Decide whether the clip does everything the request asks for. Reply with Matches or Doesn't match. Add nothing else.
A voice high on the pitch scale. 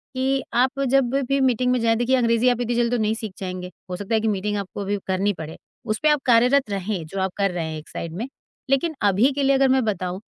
Matches